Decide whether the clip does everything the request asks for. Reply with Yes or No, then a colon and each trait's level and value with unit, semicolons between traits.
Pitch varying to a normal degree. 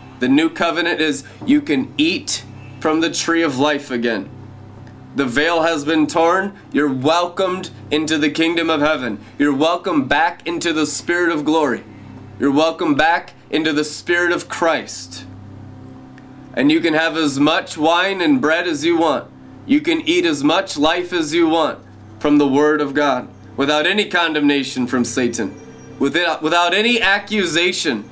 Yes: average, 4.3 semitones